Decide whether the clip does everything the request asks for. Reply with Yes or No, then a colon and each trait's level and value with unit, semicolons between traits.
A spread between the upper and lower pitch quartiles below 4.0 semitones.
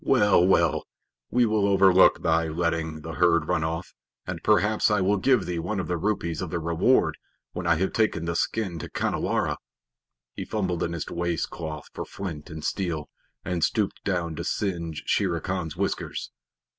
Yes: average, 2.9 semitones